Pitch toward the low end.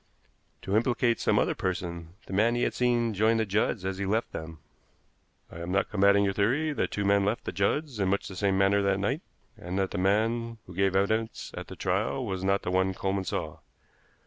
Yes: low, 100 Hz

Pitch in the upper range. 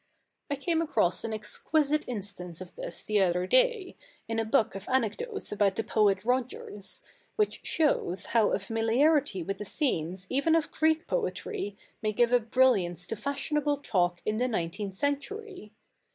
Yes: high, 225 Hz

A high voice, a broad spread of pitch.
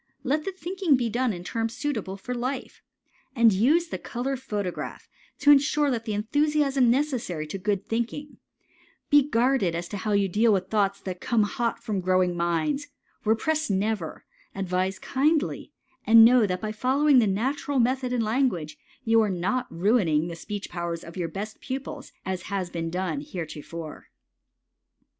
Yes: high, 220 Hz; wide, 6.1 semitones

